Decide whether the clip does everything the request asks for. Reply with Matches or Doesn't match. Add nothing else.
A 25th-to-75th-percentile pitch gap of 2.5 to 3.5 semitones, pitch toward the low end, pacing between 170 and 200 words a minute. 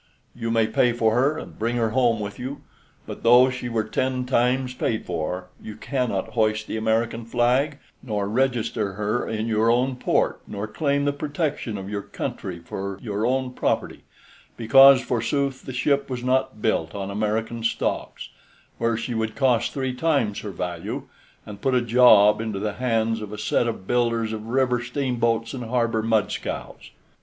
Matches